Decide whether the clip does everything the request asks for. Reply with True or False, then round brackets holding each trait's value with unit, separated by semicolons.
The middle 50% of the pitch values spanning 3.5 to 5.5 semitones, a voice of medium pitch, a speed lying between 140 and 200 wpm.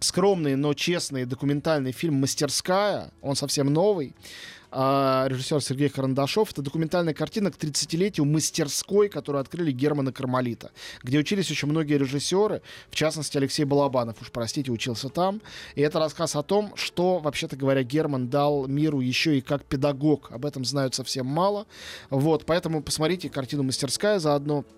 False (2.8 semitones; 145 Hz; 150 wpm)